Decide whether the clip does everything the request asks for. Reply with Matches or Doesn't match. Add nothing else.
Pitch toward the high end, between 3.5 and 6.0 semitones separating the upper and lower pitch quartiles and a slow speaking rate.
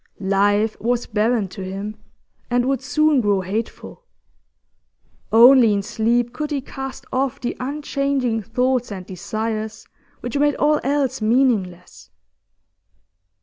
Matches